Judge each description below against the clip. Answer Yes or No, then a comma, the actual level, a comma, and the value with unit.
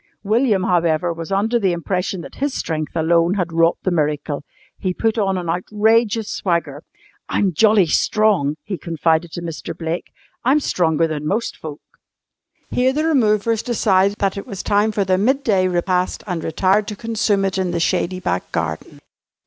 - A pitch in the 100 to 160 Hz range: No, medium, 185 Hz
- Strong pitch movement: No, average, 4.2 semitones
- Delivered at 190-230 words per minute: No, average, 170 wpm